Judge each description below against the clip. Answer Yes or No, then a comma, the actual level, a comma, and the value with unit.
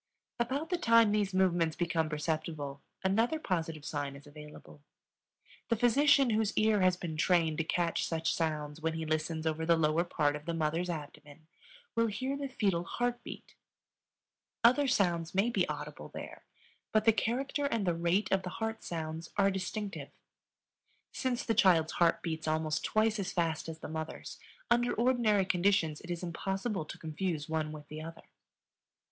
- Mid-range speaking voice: Yes, medium, 175 Hz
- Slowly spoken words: No, average, 170 wpm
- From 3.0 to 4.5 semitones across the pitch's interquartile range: No, average, 5.3 semitones